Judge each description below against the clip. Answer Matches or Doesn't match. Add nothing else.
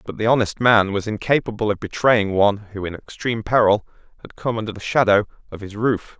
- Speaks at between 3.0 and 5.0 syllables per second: Doesn't match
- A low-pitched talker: Matches